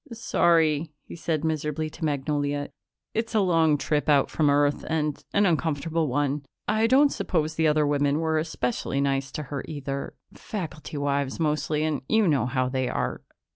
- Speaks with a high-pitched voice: No, medium, 150 Hz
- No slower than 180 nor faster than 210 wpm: No, average, 170 wpm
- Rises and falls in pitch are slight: Yes, narrow, 2.2 semitones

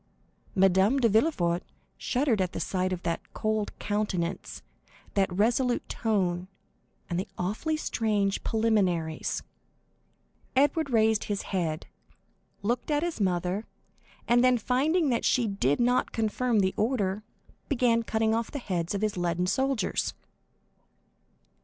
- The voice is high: Yes, high, 215 Hz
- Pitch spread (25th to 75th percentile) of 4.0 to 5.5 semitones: Yes, average, 4.7 semitones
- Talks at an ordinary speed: No, slow, 130 wpm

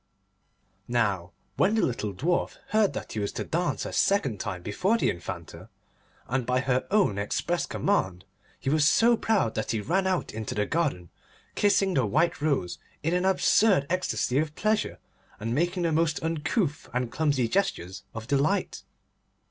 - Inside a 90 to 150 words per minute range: No, average, 165 wpm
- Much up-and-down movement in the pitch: Yes, wide, 8.7 semitones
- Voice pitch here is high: No, medium, 150 Hz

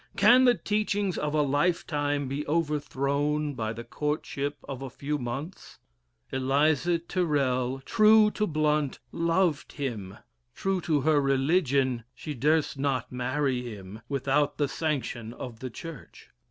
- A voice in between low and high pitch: Yes, medium, 145 Hz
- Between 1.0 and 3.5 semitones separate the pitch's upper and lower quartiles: Yes, average, 3.2 semitones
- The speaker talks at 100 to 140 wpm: Yes, slow, 135 wpm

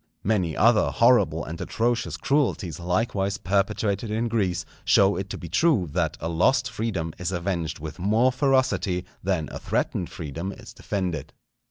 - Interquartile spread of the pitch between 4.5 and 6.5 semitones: Yes, average, 4.8 semitones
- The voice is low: Yes, very low, 95 Hz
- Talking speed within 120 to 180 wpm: Yes, average, 155 wpm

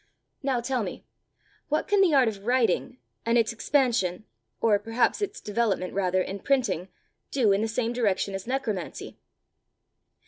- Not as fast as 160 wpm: Yes, average, 150 wpm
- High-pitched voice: Yes, high, 230 Hz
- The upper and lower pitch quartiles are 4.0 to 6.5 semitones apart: Yes, average, 4.3 semitones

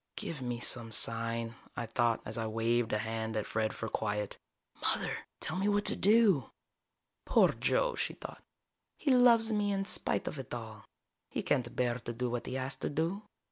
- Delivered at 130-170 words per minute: No, average, 190 wpm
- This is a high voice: No, low, 120 Hz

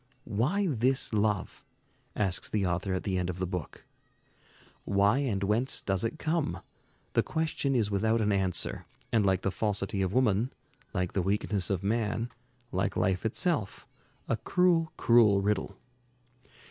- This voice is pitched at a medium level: No, low, 105 Hz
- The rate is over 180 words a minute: No, average, 150 wpm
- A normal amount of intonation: Yes, average, 3.9 semitones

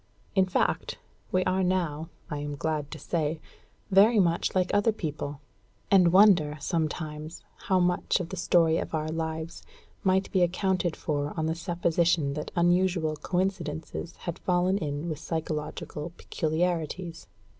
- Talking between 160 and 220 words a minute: No, average, 145 wpm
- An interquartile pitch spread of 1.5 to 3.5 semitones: Yes, average, 2.9 semitones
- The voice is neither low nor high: Yes, medium, 170 Hz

